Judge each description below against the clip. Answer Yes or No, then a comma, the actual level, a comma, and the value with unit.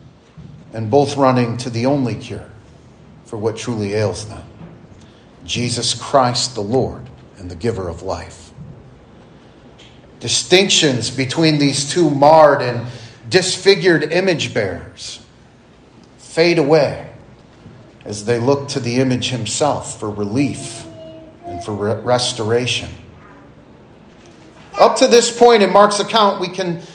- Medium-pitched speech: No, low, 125 Hz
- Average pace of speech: No, slow, 120 wpm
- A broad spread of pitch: Yes, wide, 5.8 semitones